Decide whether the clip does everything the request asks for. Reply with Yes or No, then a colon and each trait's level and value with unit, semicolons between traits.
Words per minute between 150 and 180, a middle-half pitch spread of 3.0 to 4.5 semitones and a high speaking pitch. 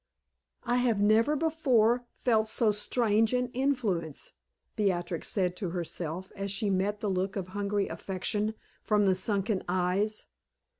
No: average, 140 wpm; average, 3.3 semitones; high, 205 Hz